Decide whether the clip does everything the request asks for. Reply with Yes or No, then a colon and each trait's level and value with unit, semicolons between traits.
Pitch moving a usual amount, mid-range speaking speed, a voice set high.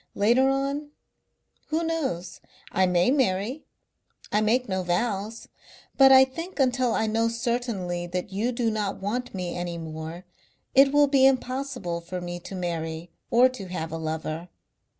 No: wide, 6.8 semitones; average, 155 wpm; high, 215 Hz